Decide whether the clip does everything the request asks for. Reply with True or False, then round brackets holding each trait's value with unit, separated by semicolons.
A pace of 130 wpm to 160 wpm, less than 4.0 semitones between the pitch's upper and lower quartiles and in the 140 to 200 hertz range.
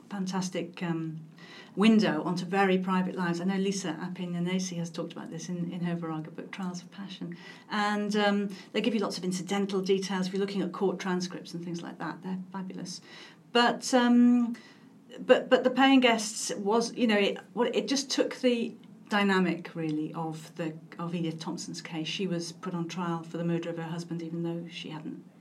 False (195 wpm; 3.5 semitones; 185 Hz)